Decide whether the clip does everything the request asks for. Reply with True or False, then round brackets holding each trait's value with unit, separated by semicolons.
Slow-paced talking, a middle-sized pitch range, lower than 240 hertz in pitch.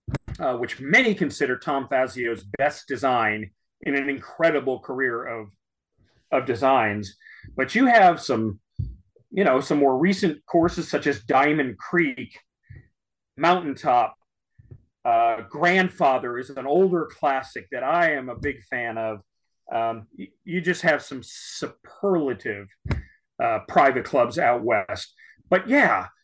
False (130 wpm; 7.1 semitones; 140 Hz)